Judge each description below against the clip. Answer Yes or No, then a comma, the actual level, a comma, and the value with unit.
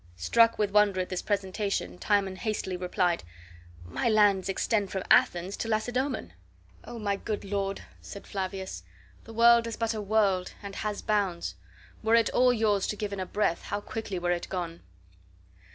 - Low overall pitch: No, high, 200 Hz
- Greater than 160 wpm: Yes, average, 170 wpm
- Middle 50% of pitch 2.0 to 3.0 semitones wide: Yes, narrow, 2.6 semitones